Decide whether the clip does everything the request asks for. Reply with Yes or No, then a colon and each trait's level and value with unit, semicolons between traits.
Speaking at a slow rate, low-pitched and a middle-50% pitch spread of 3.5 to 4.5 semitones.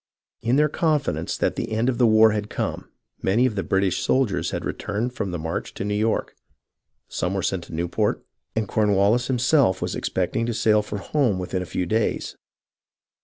No: average, 195 wpm; low, 110 Hz; average, 3.8 semitones